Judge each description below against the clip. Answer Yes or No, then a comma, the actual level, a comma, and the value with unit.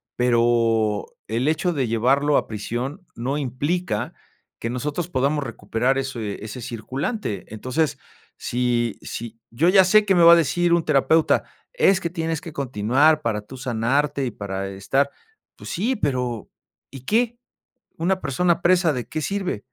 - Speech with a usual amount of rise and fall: No, wide, 6.1 semitones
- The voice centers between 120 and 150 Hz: Yes, low, 135 Hz